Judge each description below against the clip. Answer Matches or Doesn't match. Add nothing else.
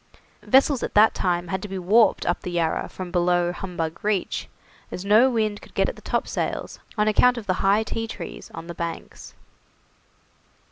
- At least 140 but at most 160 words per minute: Doesn't match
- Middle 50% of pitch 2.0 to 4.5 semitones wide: Matches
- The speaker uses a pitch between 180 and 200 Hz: Matches